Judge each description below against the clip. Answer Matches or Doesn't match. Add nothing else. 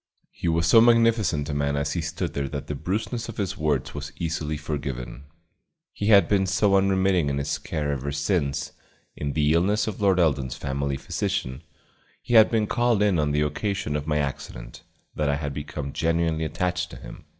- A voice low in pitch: Matches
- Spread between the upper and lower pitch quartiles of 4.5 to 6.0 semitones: Matches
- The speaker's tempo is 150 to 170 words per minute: Doesn't match